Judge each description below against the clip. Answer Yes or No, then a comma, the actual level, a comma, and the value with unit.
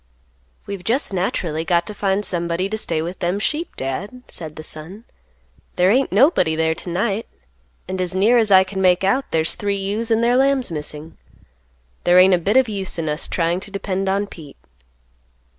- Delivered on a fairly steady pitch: No, average, 3.6 semitones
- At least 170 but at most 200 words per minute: Yes, average, 190 wpm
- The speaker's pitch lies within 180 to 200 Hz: Yes, high, 190 Hz